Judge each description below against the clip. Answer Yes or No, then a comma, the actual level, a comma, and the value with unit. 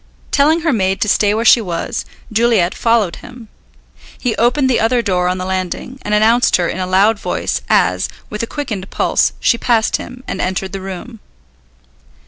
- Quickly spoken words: No, average, 185 wpm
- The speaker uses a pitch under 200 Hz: No, high, 215 Hz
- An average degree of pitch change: Yes, average, 4.2 semitones